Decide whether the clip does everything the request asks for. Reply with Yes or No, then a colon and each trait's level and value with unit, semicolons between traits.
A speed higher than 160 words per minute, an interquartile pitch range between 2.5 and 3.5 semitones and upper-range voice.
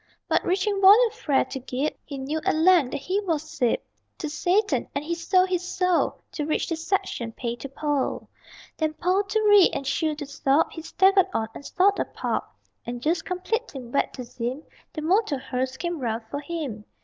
No: average, 195 wpm; wide, 5.4 semitones; very high, 315 Hz